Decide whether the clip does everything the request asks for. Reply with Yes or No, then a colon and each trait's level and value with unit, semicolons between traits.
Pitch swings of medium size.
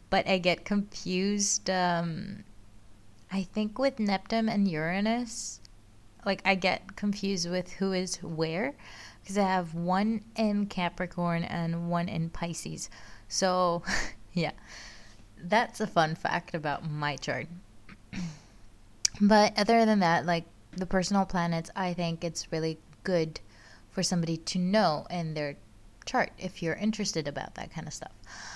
Yes: average, 3.8 semitones